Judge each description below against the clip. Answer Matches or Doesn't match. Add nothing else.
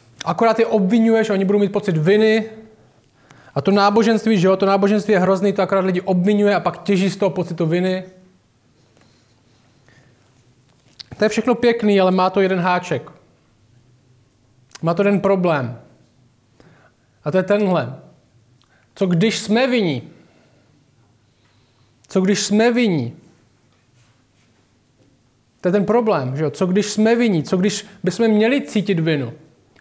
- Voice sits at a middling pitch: Matches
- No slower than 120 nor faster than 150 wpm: Matches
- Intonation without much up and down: Doesn't match